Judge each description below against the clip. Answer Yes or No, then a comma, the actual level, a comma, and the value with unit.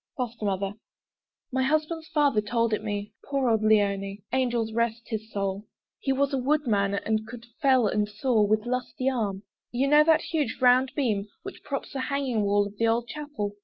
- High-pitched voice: Yes, high, 230 Hz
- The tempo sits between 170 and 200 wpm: Yes, average, 185 wpm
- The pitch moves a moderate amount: Yes, average, 4.3 semitones